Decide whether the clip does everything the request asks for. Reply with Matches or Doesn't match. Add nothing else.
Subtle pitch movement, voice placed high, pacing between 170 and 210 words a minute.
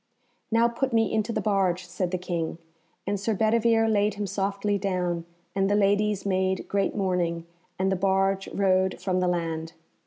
Matches